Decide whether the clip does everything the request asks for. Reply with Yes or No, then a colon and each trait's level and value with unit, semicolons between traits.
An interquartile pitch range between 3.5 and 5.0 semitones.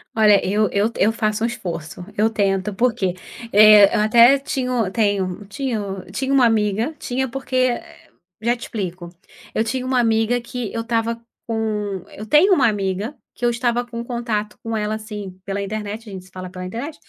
No: average, 3.0 semitones